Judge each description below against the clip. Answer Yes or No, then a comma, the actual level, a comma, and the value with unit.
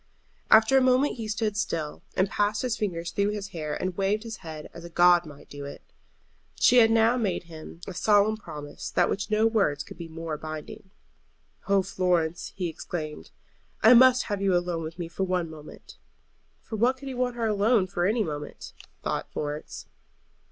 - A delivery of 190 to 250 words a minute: Yes, average, 195 wpm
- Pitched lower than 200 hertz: Yes, high, 190 Hz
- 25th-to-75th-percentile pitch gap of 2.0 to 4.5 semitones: No, average, 4.9 semitones